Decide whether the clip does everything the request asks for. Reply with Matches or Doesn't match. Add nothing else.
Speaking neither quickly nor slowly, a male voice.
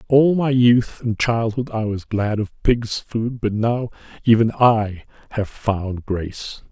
Matches